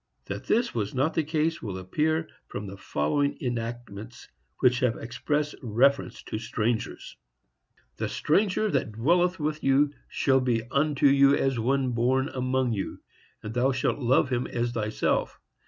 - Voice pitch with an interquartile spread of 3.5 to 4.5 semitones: Yes, average, 3.9 semitones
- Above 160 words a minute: No, average, 155 wpm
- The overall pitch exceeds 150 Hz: No, low, 130 Hz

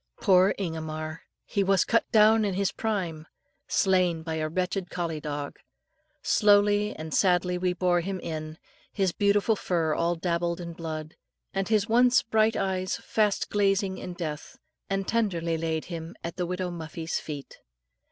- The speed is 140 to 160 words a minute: Yes, average, 155 wpm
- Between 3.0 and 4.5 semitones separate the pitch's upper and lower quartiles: Yes, average, 3.4 semitones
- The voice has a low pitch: No, medium, 180 Hz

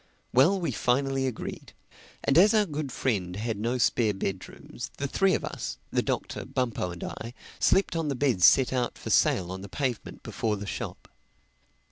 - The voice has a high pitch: No, low, 125 Hz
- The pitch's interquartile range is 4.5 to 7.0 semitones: Yes, wide, 5.4 semitones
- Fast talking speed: No, average, 180 wpm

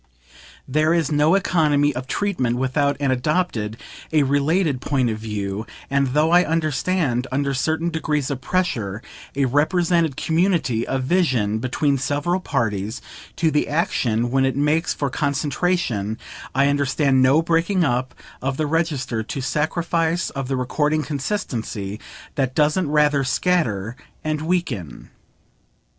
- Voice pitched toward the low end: No, medium, 145 Hz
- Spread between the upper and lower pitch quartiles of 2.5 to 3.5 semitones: No, average, 4.2 semitones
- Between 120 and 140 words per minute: Yes, slow, 135 wpm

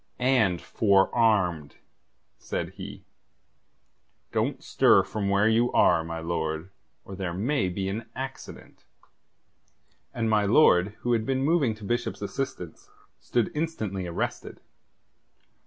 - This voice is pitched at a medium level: No, low, 105 Hz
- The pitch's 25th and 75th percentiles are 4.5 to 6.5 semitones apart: Yes, average, 4.9 semitones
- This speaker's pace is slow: Yes, slow, 120 wpm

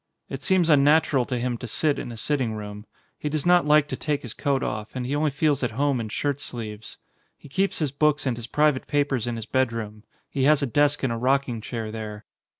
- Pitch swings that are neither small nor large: Yes, average, 4.2 semitones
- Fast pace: Yes, fast, 235 wpm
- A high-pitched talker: No, low, 135 Hz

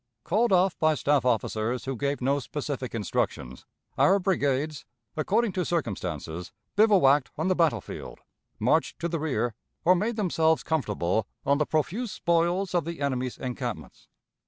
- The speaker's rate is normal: Yes, average, 150 wpm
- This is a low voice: No, medium, 150 Hz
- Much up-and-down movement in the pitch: Yes, wide, 5.8 semitones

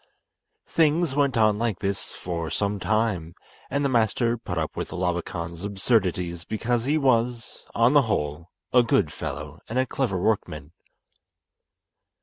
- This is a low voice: Yes, low, 110 Hz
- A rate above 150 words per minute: No, average, 140 wpm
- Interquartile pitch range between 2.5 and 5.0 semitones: No, wide, 5.6 semitones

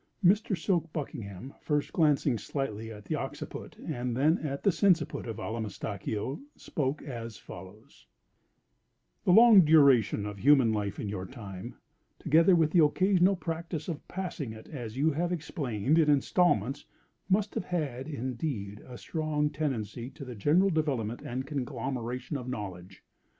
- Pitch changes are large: Yes, wide, 6.1 semitones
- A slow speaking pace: No, average, 145 wpm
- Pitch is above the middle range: No, medium, 140 Hz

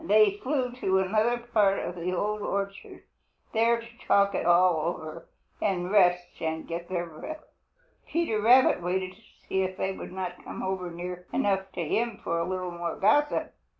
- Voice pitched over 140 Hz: Yes, high, 190 Hz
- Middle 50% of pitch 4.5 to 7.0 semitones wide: No, average, 3.2 semitones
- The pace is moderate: Yes, average, 180 wpm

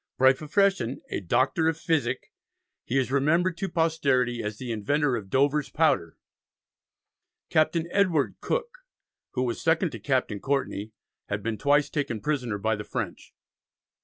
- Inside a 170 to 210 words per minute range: No, average, 145 wpm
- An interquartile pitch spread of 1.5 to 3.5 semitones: No, wide, 5.4 semitones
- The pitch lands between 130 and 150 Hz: Yes, medium, 140 Hz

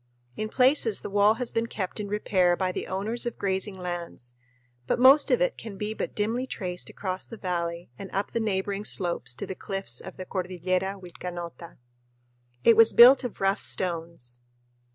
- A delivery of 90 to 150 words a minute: No, average, 180 wpm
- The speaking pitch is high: Yes, high, 195 Hz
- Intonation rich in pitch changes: No, average, 3.5 semitones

